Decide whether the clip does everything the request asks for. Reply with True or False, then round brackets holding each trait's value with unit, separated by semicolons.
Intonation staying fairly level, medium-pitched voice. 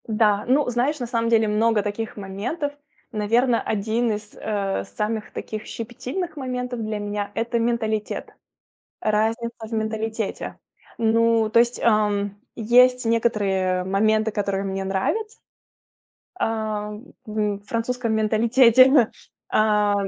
False (2.1 semitones; 220 Hz)